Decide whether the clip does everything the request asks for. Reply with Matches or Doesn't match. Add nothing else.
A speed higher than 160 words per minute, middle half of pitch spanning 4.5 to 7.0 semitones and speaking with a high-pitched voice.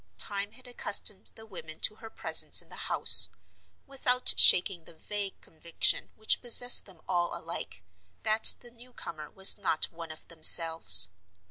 Doesn't match